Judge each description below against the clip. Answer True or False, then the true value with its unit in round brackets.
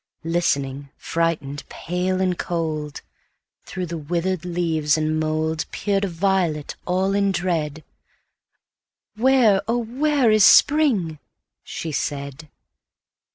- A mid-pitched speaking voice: True (170 Hz)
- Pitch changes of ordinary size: True (3.9 semitones)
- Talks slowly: True (95 wpm)